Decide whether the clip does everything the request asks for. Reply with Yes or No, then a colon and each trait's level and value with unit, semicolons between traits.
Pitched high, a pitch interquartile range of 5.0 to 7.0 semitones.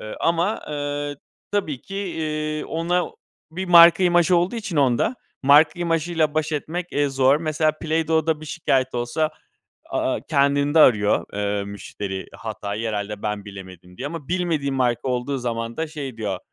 No: medium, 145 Hz; wide, 5.4 semitones